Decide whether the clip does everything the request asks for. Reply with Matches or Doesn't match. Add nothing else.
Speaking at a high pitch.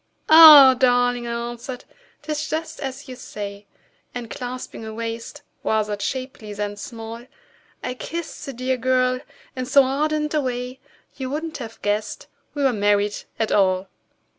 Matches